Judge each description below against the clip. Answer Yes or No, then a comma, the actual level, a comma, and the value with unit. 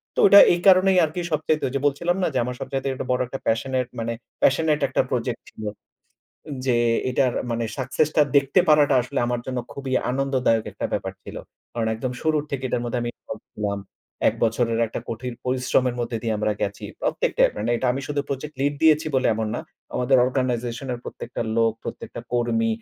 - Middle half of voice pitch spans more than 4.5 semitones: No, average, 3.2 semitones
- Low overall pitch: Yes, low, 130 Hz